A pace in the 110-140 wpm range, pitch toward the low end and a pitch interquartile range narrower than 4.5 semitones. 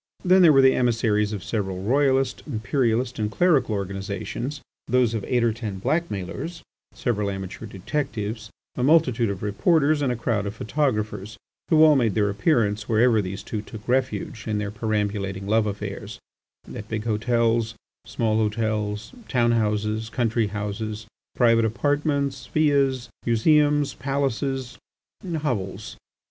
Yes: slow, 135 wpm; low, 115 Hz; average, 4.1 semitones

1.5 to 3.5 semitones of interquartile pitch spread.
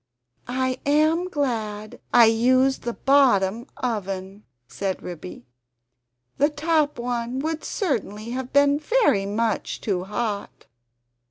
No: average, 5.3 semitones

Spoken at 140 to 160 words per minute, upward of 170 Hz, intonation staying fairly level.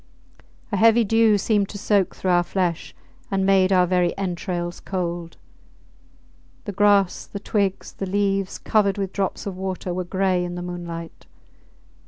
Yes: average, 155 wpm; high, 190 Hz; narrow, 2.1 semitones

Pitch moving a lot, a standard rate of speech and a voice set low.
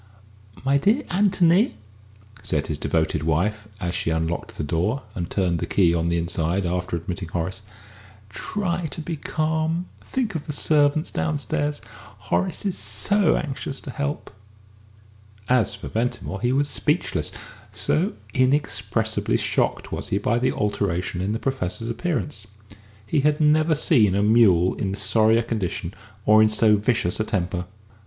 Yes: wide, 8.5 semitones; average, 150 wpm; low, 110 Hz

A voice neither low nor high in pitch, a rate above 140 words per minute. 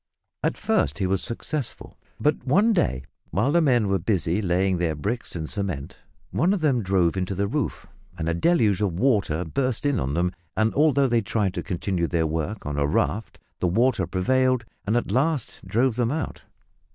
No: low, 105 Hz; average, 190 wpm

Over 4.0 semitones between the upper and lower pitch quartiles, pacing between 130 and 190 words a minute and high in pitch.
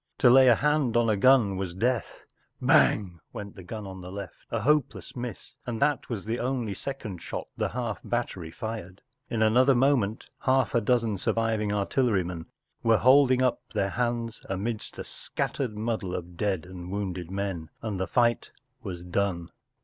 No: average, 4.4 semitones; average, 180 wpm; low, 110 Hz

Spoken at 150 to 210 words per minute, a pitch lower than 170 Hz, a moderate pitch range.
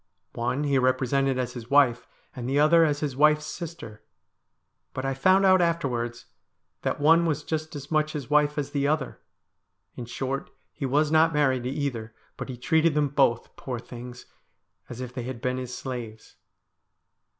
Yes: average, 175 wpm; medium, 140 Hz; average, 3.4 semitones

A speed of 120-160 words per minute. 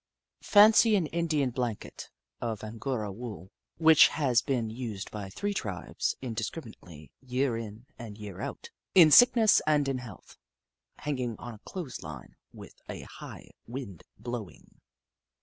Yes: average, 140 wpm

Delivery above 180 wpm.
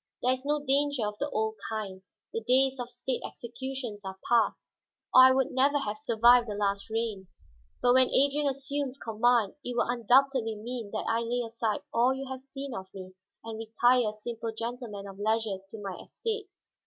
Yes: average, 190 wpm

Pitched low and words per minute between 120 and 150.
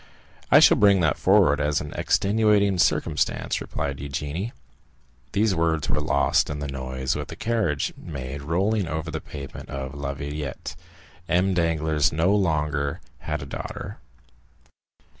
Yes: very low, 75 Hz; average, 145 wpm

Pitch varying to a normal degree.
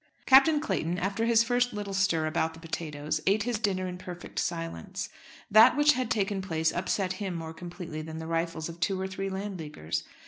Yes: average, 4.0 semitones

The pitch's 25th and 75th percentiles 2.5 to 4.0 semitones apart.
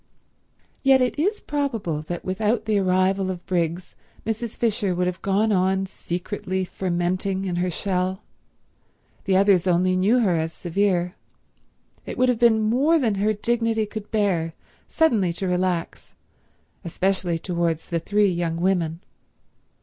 Yes: average, 3.5 semitones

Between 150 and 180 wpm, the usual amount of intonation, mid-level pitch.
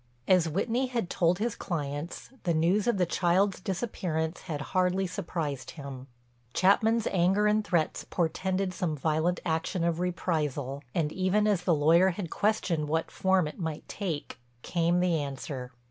Yes: average, 155 wpm; average, 3.3 semitones; medium, 175 Hz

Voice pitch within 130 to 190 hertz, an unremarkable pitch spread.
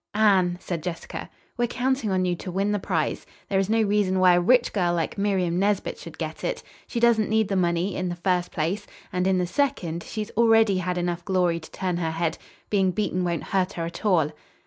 Yes: medium, 185 Hz; average, 3.0 semitones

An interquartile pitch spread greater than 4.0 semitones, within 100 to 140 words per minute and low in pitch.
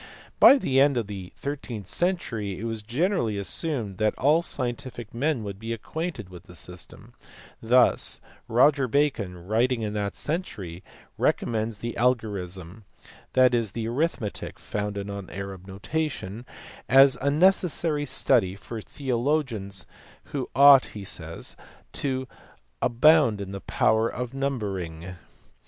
Yes: wide, 5.6 semitones; slow, 135 wpm; low, 115 Hz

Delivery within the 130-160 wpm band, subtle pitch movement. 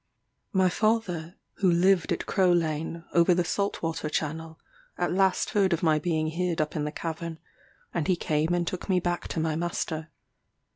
No: average, 185 wpm; narrow, 2.2 semitones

